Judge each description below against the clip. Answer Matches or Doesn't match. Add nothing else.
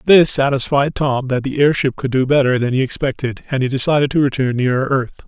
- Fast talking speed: Matches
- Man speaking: Matches